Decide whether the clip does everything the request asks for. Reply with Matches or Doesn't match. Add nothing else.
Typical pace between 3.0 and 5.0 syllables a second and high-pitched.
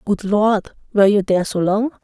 Doesn't match